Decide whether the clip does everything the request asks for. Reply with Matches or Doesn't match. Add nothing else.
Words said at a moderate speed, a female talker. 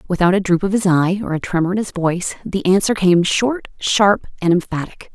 Doesn't match